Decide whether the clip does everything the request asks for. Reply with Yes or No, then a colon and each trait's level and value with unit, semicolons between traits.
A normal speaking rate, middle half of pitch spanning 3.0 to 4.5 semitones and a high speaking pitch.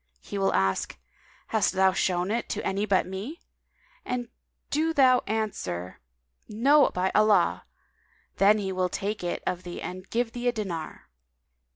Yes: average, 155 wpm; average, 4.2 semitones; high, 200 Hz